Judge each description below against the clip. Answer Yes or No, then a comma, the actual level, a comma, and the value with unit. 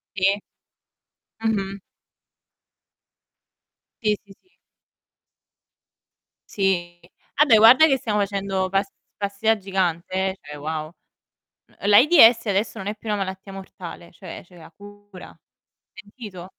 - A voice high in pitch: Yes, high, 195 Hz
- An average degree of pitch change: No, narrow, 2.1 semitones